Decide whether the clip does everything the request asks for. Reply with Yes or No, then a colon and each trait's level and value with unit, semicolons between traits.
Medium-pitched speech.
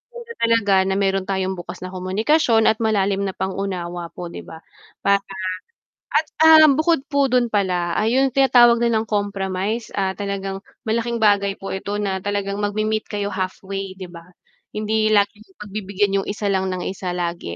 No: high, 200 Hz